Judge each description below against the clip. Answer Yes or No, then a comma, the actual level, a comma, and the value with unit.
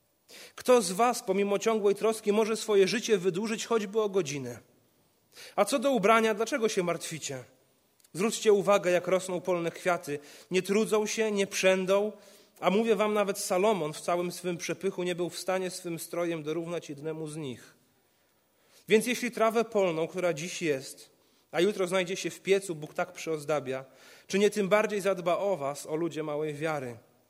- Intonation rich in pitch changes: No, average, 4.4 semitones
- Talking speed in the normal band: No, fast, 170 wpm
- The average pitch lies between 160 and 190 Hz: Yes, medium, 185 Hz